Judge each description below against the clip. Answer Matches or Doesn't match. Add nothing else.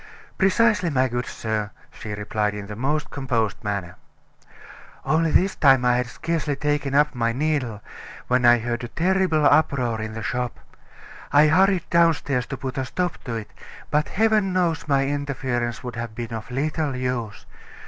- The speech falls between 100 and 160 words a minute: Doesn't match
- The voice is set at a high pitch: Doesn't match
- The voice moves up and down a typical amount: Matches